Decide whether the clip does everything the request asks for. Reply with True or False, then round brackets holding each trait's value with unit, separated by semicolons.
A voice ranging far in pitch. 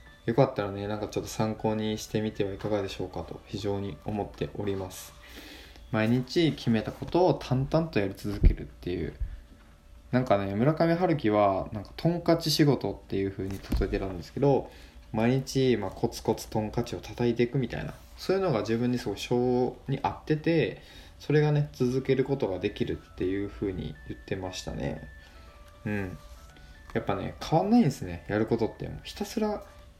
True (6.6 semitones)